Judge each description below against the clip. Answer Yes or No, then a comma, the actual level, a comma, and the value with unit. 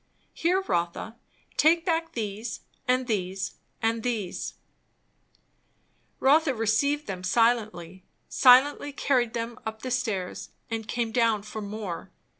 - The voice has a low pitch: No, high, 230 Hz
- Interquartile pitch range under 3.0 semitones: No, average, 3.6 semitones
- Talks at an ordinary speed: No, slow, 115 wpm